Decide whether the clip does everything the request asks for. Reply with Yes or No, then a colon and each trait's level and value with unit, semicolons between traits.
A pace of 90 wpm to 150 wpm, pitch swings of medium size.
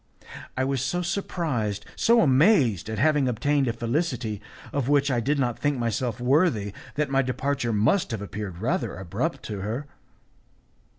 No: average, 160 wpm; average, 4.7 semitones